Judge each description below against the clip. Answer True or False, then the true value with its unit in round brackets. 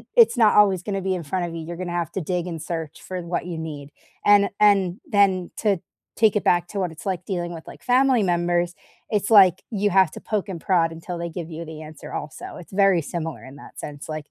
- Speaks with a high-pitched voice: False (175 Hz)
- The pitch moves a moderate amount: True (3.2 semitones)